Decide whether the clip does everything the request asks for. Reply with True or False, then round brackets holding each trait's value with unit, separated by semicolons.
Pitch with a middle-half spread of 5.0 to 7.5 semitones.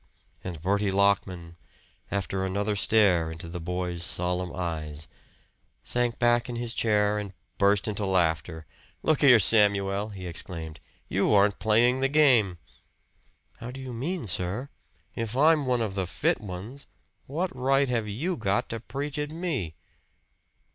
True (5.3 semitones)